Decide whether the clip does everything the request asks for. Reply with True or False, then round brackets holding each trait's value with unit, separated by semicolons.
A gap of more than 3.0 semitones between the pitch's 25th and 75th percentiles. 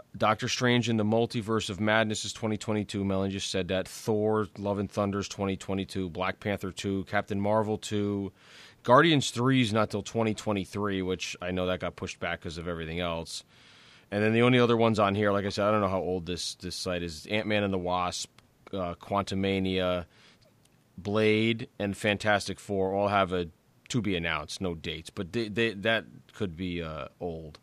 False (2.7 semitones)